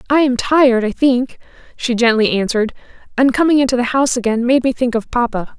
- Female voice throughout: Yes, female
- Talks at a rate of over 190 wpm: Yes, fast, 205 wpm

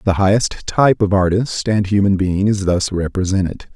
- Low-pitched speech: Yes, low, 100 Hz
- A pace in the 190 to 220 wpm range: No, average, 175 wpm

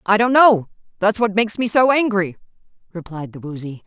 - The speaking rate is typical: Yes, average, 185 wpm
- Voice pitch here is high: Yes, high, 200 Hz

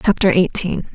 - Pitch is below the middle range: No, medium, 185 Hz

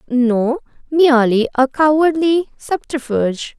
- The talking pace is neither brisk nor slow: No, slow, 85 wpm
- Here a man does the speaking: No, female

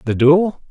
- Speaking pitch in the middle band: Yes, medium, 155 Hz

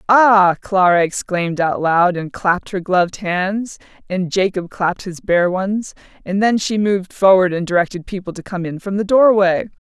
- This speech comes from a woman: Yes, female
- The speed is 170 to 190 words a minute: Yes, average, 180 wpm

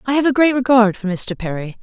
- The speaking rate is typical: No, fast, 265 wpm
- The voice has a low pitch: No, high, 230 Hz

